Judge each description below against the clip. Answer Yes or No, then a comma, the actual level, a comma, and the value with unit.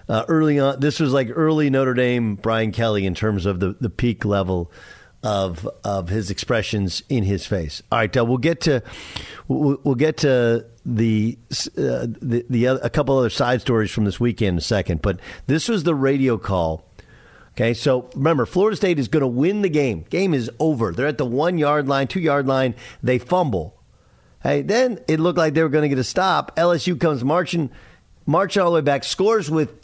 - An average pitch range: No, wide, 6.2 semitones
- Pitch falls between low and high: No, low, 125 Hz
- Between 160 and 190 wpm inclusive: No, fast, 205 wpm